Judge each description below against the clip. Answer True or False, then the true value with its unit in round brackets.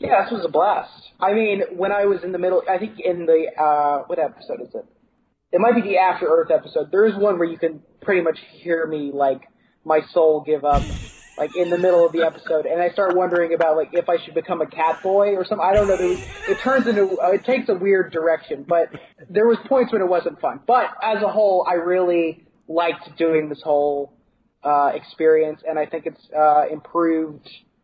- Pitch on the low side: False (170 Hz)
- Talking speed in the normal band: False (220 wpm)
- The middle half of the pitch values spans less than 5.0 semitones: True (3.9 semitones)